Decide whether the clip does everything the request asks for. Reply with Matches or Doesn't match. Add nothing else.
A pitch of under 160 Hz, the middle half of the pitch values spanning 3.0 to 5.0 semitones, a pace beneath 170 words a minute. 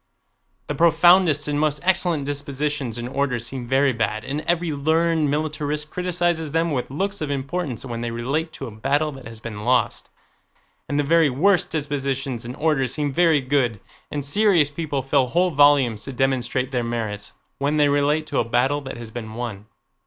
Doesn't match